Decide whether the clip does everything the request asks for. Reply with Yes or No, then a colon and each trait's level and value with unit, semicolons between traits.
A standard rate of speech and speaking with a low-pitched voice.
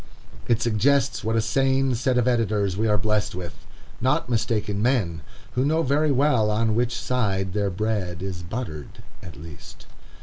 Yes: average, 165 wpm; low, 110 Hz